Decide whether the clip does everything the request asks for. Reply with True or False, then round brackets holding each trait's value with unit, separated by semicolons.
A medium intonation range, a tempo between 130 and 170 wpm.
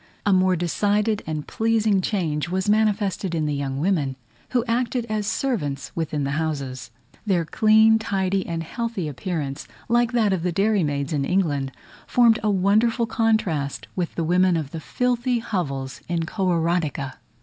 False (6.0 semitones; 160 wpm)